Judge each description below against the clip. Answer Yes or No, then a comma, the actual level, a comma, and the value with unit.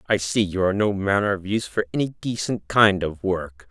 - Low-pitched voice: Yes, low, 100 Hz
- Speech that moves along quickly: Yes, fast, 225 wpm